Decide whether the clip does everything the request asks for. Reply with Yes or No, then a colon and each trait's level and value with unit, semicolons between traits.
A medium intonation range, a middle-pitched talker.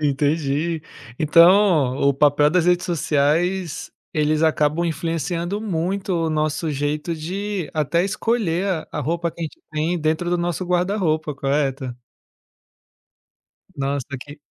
Yes: average, 3.0 semitones; medium, 160 Hz